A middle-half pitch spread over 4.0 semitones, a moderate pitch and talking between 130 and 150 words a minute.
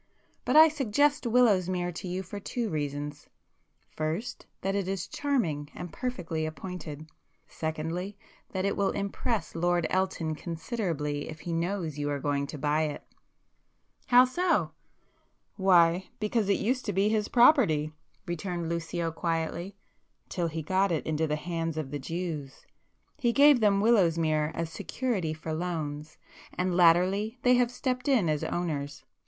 Yes: average, 4.6 semitones; medium, 175 Hz; average, 140 wpm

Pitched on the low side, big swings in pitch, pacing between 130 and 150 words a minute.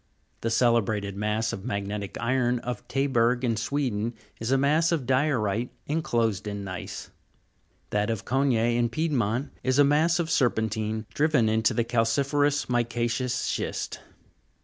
No: low, 120 Hz; average, 3.6 semitones; average, 140 wpm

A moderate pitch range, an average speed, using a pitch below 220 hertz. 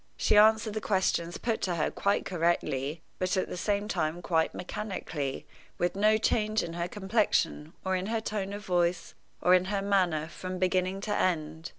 Yes: average, 3.3 semitones; average, 185 wpm; medium, 185 Hz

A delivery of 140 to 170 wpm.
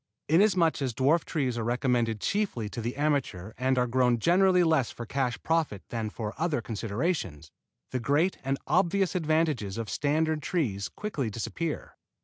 Yes: average, 155 wpm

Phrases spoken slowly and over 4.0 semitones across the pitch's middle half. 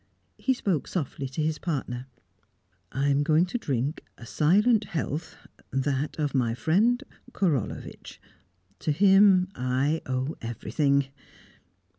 Yes: slow, 120 wpm; wide, 5.4 semitones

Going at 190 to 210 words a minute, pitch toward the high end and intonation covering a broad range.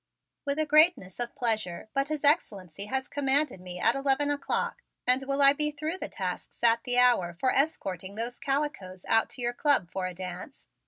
Yes: average, 195 wpm; very high, 250 Hz; wide, 6.9 semitones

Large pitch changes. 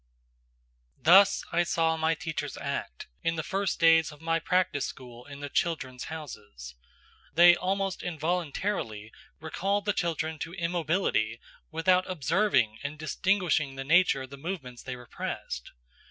No: average, 4.7 semitones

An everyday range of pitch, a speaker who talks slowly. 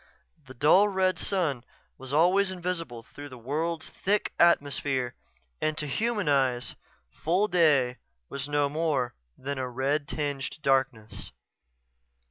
Yes: average, 4.5 semitones; slow, 125 wpm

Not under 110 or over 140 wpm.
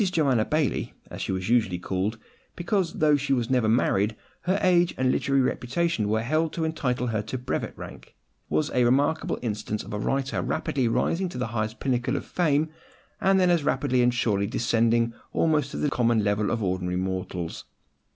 No: average, 185 wpm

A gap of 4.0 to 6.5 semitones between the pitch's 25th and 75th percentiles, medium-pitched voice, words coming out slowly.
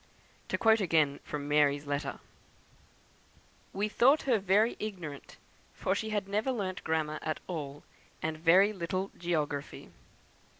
Yes: wide, 5.5 semitones; medium, 175 Hz; slow, 130 wpm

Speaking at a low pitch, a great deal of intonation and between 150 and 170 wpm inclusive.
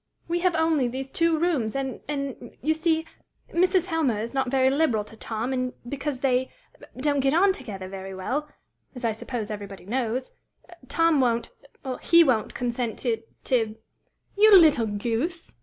No: very high, 260 Hz; wide, 5.7 semitones; average, 165 wpm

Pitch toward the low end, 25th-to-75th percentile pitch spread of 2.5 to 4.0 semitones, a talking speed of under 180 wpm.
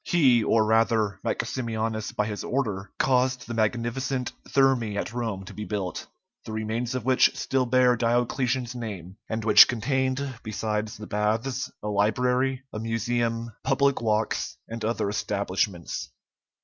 Yes: low, 115 Hz; average, 2.9 semitones; average, 140 wpm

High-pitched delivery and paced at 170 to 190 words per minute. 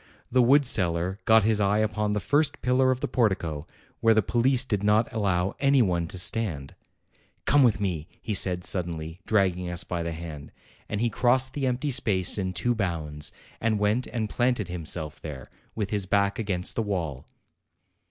No: low, 100 Hz; average, 180 wpm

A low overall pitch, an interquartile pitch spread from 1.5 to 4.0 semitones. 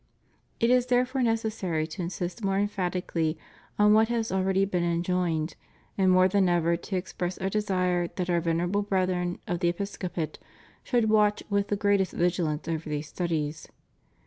No: medium, 185 Hz; average, 2.9 semitones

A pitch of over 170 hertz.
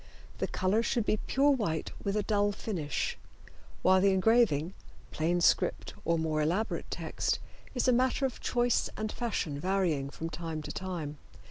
Yes: high, 190 Hz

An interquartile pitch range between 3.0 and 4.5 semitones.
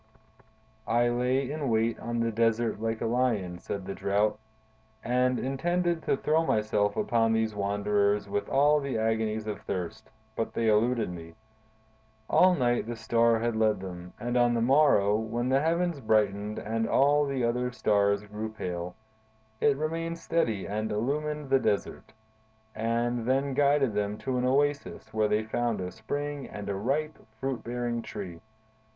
Yes: average, 4.1 semitones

